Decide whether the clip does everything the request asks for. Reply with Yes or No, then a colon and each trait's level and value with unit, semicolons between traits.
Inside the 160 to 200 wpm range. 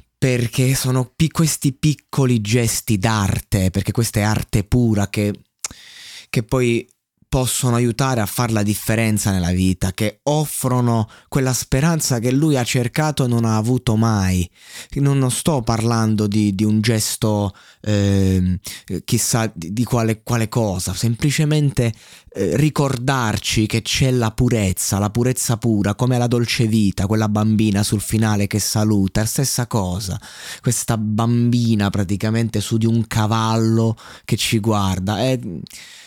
No: average, 140 wpm